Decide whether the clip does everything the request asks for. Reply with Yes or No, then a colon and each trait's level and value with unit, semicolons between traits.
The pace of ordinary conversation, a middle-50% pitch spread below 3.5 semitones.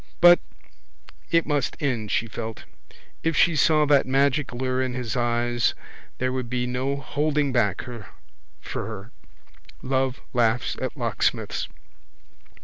No: slow, 130 wpm; average, 2.9 semitones